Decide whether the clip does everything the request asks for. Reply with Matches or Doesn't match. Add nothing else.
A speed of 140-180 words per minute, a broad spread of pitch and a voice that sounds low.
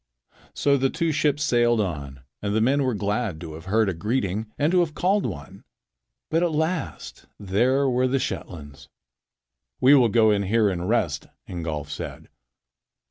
Matches